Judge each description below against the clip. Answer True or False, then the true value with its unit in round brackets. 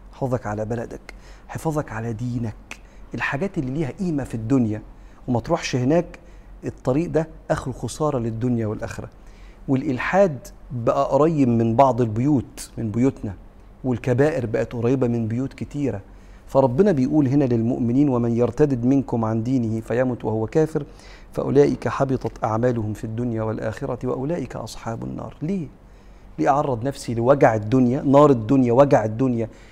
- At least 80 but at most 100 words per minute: False (135 wpm)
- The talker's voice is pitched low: True (125 Hz)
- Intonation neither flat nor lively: True (3.8 semitones)